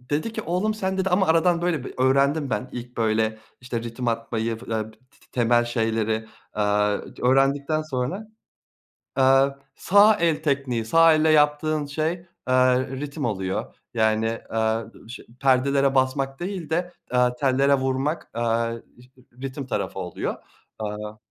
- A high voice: No, low, 130 Hz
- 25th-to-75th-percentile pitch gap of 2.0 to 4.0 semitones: No, average, 5.2 semitones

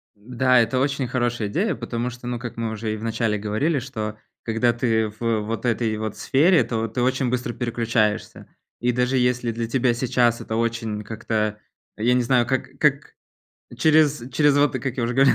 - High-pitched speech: No, low, 120 Hz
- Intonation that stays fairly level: Yes, narrow, 2.3 semitones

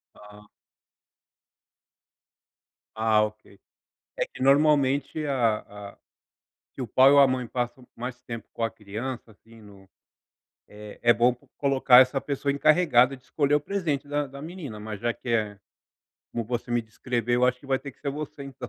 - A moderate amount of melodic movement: Yes, average, 3.8 semitones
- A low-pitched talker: Yes, low, 125 Hz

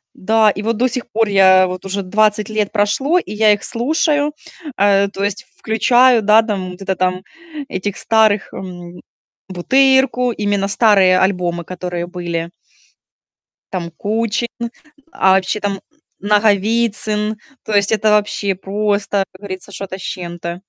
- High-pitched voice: Yes, high, 205 Hz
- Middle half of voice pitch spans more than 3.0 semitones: No, average, 2.7 semitones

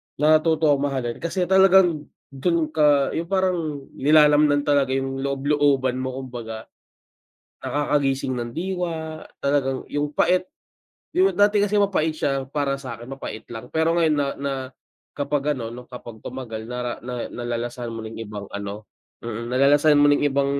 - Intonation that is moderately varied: Yes, average, 3.9 semitones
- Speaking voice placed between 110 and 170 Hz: Yes, medium, 140 Hz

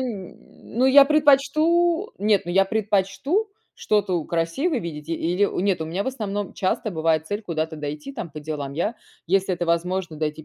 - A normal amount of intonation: No, wide, 6.3 semitones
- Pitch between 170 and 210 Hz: Yes, high, 190 Hz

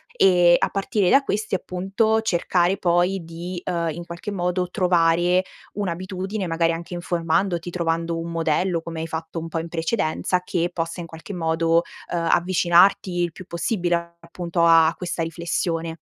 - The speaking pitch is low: No, medium, 175 Hz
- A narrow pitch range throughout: Yes, narrow, 1.7 semitones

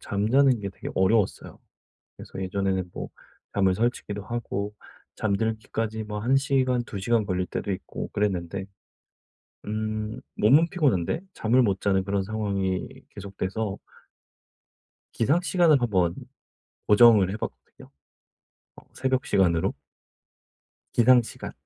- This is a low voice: Yes, low, 105 Hz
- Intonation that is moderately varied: Yes, average, 3.6 semitones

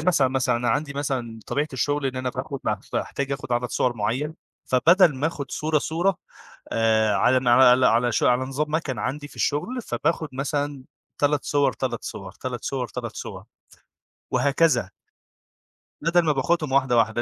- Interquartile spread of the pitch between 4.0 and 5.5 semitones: No, average, 3.3 semitones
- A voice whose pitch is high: No, low, 135 Hz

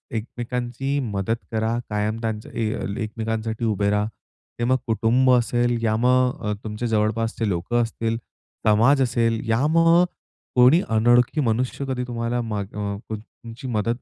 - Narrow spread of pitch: Yes, narrow, 2.0 semitones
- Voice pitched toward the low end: Yes, low, 115 Hz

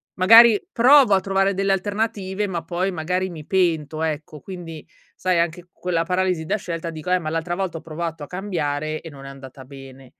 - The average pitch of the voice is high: No, medium, 175 Hz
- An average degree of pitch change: Yes, average, 3.4 semitones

